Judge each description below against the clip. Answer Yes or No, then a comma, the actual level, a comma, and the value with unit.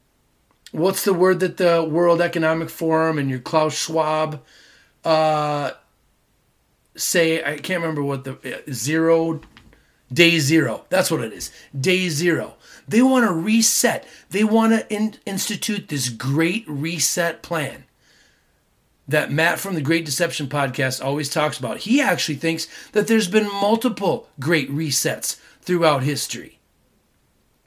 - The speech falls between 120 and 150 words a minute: Yes, slow, 135 wpm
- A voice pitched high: No, medium, 165 Hz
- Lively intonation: No, average, 4.2 semitones